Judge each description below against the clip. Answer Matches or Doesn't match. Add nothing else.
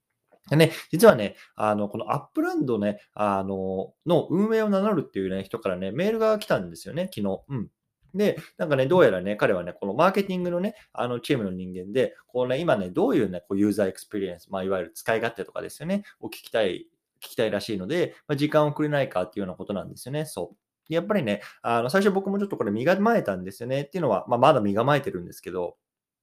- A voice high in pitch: Doesn't match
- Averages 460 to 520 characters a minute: Matches